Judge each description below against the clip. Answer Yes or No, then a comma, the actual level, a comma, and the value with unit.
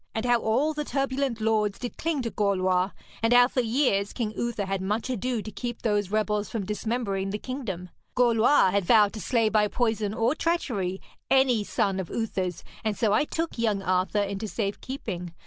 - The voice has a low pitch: No, high, 220 Hz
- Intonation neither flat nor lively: Yes, average, 3.6 semitones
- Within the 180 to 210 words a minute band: Yes, average, 190 wpm